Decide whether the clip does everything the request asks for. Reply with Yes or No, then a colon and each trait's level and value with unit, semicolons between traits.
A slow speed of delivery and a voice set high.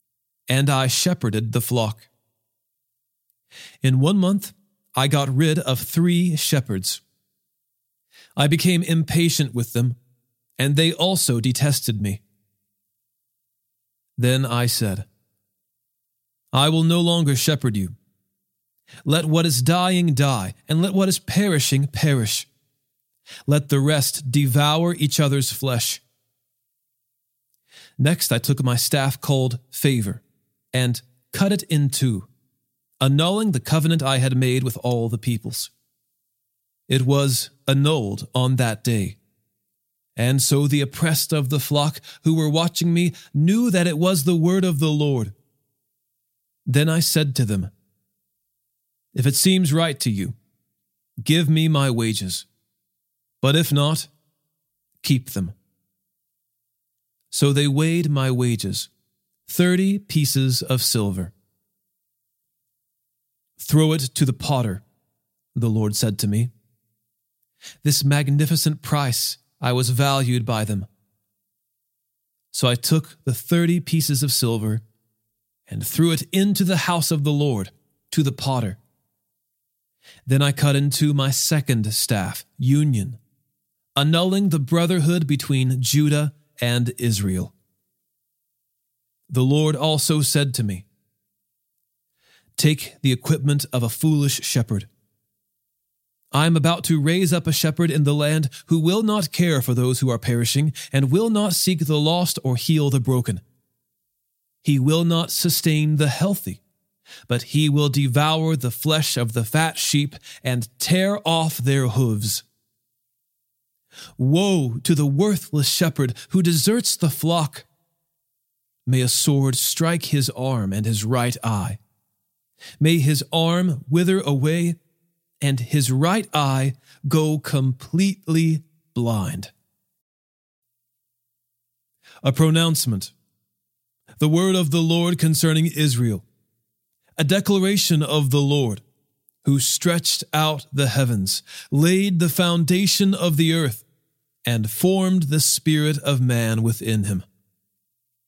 No: slow, 125 wpm; low, 135 Hz